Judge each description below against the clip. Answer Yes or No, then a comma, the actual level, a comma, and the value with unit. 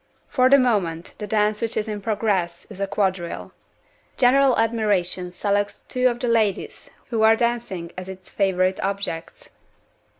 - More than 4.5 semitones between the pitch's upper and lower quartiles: No, average, 3.6 semitones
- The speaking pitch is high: Yes, high, 205 Hz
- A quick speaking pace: No, average, 155 wpm